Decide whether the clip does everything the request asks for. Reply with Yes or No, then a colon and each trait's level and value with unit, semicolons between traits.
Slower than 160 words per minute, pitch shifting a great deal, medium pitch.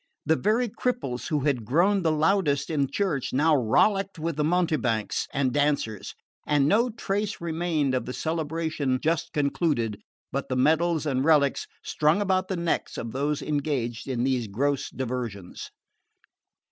No: average, 150 wpm; average, 4.5 semitones; medium, 150 Hz